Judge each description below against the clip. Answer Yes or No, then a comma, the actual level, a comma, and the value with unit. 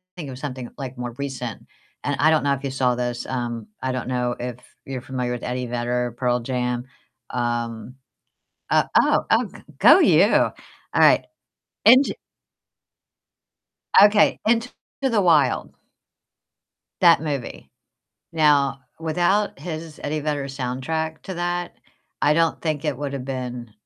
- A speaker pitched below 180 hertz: Yes, low, 135 Hz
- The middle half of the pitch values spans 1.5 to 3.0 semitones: No, average, 4.2 semitones